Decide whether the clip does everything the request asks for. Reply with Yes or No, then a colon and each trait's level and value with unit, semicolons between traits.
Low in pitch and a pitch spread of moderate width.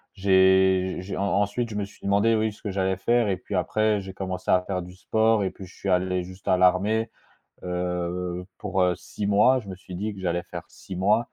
No: very low, 95 Hz; narrow, 2.2 semitones